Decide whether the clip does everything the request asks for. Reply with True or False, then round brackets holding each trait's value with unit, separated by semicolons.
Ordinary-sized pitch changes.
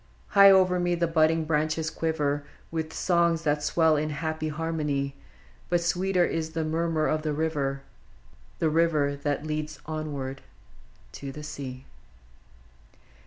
False (2.0 semitones)